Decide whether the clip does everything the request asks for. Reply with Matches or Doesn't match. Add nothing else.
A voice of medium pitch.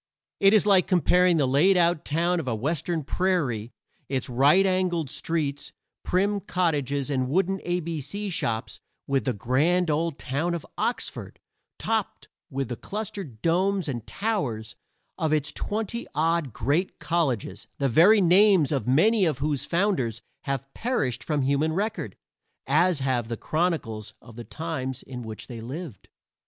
Matches